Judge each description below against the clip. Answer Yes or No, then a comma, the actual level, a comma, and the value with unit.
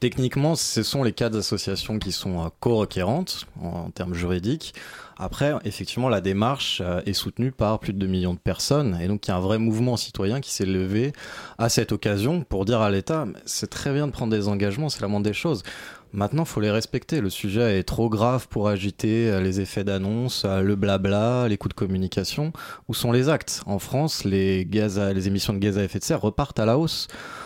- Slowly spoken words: No, average, 210 wpm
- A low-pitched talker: Yes, low, 105 Hz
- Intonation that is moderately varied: Yes, average, 4.0 semitones